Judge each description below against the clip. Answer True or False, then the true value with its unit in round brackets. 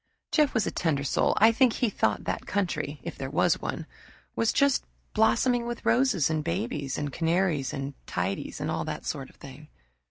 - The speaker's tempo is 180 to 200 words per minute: True (190 wpm)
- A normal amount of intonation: False (8.2 semitones)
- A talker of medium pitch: True (170 Hz)